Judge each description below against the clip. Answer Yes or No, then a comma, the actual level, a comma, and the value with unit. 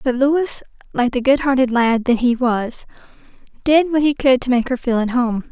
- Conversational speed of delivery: No, fast, 220 wpm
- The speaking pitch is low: No, very high, 255 Hz